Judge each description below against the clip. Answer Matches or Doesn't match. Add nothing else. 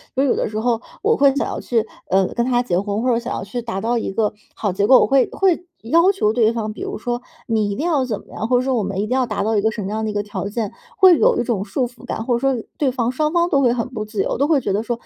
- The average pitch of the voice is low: Doesn't match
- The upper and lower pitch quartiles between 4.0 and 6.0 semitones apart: Doesn't match